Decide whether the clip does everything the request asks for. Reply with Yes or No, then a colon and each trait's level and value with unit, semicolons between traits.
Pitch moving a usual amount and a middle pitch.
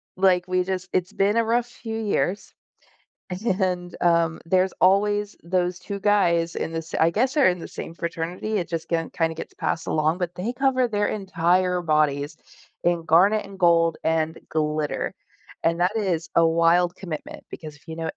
Yes: average, 3.1 semitones; medium, 175 Hz